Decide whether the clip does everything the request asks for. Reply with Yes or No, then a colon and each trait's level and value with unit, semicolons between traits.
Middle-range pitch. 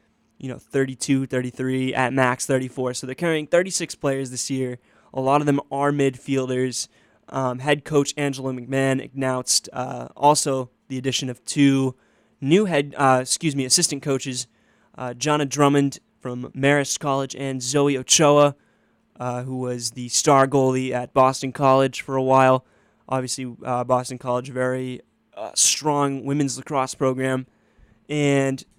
No: low, 130 Hz